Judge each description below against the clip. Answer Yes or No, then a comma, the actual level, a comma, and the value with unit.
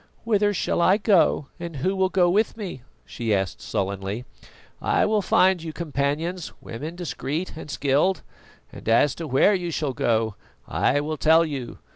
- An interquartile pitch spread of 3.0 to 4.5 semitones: No, wide, 5.5 semitones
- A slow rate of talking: No, average, 165 wpm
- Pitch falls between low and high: Yes, medium, 160 Hz